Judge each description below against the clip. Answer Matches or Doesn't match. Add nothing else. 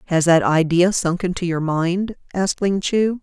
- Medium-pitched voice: Matches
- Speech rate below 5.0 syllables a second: Matches